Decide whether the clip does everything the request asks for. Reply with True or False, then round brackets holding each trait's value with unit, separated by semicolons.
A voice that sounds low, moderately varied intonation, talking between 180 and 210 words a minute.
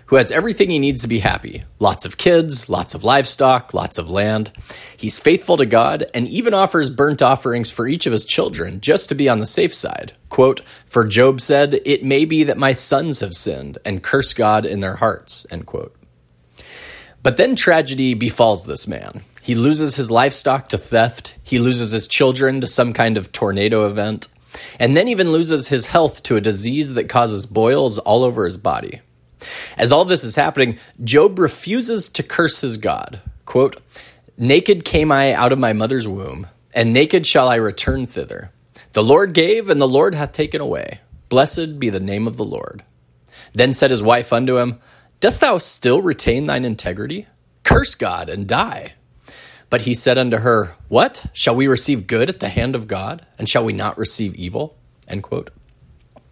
True (125 Hz; 4.6 semitones; 190 wpm)